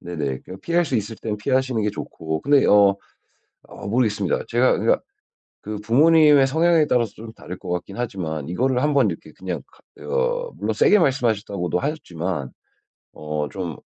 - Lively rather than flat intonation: Yes, wide, 7.6 semitones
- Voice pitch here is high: No, low, 110 Hz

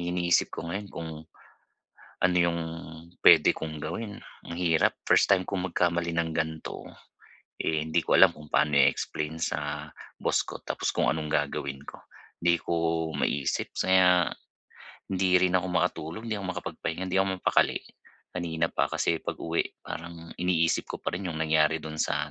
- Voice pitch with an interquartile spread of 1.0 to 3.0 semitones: Yes, narrow, 2.4 semitones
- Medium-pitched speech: No, very low, 85 Hz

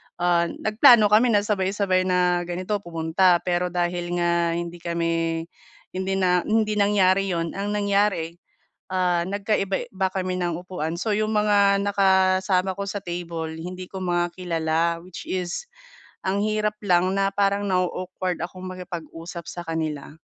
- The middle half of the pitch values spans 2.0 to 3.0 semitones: Yes, narrow, 2.4 semitones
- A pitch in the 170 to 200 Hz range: Yes, medium, 185 Hz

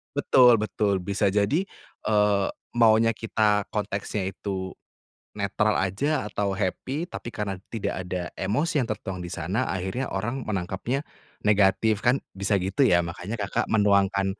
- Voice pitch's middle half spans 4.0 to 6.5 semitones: No, average, 2.9 semitones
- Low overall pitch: Yes, low, 105 Hz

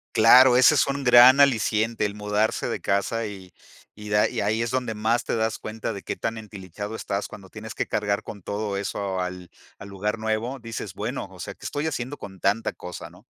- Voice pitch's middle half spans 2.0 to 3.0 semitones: Yes, narrow, 2.4 semitones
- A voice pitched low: Yes, low, 110 Hz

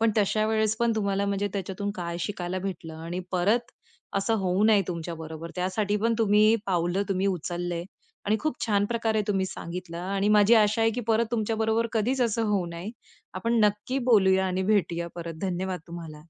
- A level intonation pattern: No, average, 3.5 semitones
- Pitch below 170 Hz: No, high, 200 Hz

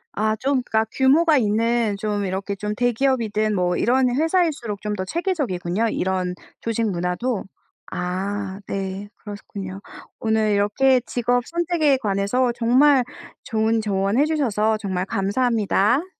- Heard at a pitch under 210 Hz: No, high, 220 Hz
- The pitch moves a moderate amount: Yes, average, 4.4 semitones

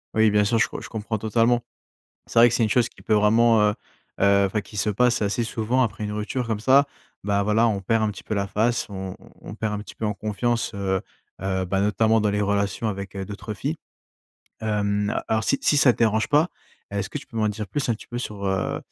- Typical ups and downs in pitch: No, narrow, 2.3 semitones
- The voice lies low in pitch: Yes, low, 105 Hz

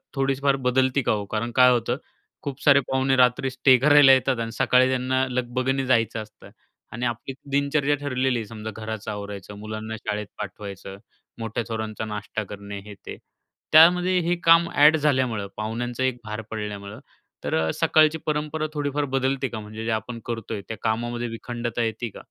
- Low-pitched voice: Yes, low, 120 Hz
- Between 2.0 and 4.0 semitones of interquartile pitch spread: Yes, average, 3.6 semitones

